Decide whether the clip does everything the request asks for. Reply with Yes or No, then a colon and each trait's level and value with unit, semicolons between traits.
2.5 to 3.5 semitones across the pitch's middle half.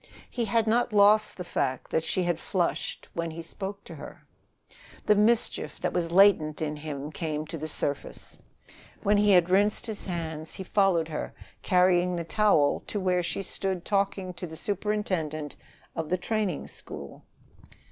No: average, 4.1 semitones